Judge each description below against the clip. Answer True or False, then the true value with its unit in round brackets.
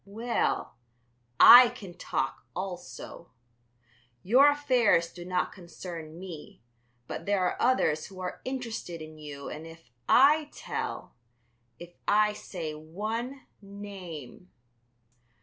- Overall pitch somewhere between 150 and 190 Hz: True (185 Hz)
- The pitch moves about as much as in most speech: False (5.9 semitones)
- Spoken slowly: True (115 wpm)